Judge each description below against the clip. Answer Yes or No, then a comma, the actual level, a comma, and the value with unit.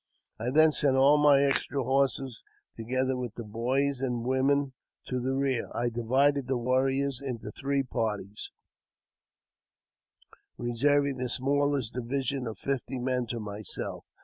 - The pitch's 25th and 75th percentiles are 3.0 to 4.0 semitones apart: No, narrow, 2.4 semitones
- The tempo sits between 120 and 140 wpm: Yes, slow, 135 wpm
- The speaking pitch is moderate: No, low, 130 Hz